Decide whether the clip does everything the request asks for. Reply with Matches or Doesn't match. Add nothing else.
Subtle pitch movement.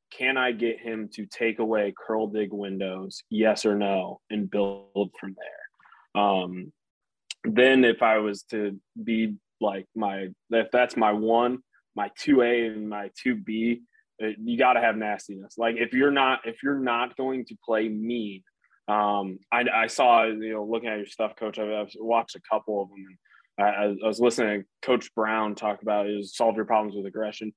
Matches